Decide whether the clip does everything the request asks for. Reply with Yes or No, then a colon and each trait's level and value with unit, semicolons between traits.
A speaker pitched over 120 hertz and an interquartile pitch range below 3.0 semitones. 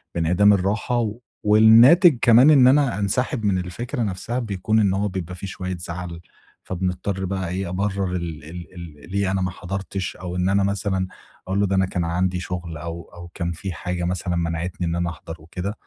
No: very low, 95 Hz; narrow, 2.6 semitones